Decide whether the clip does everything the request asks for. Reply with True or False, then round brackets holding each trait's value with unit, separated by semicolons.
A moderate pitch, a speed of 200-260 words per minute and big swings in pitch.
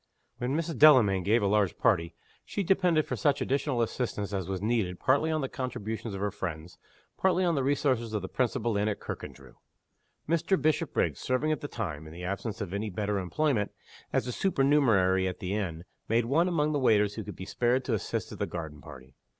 False (115 Hz; 205 wpm; 6.5 semitones)